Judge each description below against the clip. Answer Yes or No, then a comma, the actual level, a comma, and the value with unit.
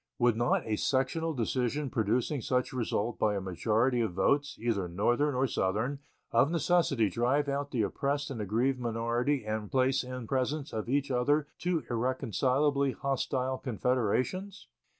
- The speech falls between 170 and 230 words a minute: No, average, 150 wpm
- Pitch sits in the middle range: No, low, 125 Hz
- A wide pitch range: No, average, 3.6 semitones